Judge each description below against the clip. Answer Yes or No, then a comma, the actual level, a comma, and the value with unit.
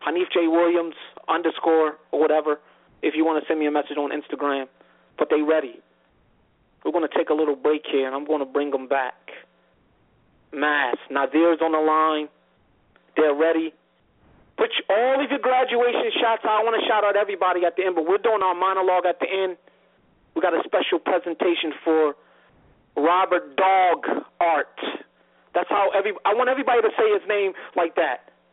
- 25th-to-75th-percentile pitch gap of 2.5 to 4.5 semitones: No, average, 4.9 semitones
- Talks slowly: No, average, 185 wpm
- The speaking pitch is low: No, medium, 165 Hz